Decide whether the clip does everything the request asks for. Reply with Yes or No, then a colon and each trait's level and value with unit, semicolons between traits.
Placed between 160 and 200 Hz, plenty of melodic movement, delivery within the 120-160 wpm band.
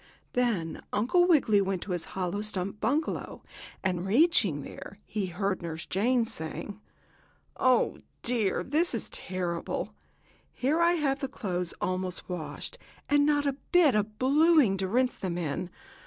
No: high, 210 Hz; wide, 6.8 semitones; average, 150 wpm